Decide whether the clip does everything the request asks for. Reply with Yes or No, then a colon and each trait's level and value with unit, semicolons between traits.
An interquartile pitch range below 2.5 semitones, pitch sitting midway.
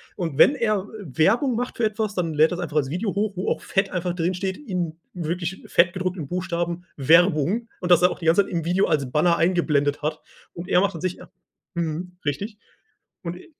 No: average, 2.8 semitones; medium, 180 Hz